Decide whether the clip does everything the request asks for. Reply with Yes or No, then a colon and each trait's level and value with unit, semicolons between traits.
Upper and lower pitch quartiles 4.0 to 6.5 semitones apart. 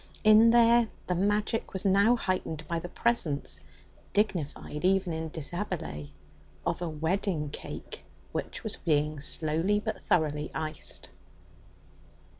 Yes: average, 5.1 semitones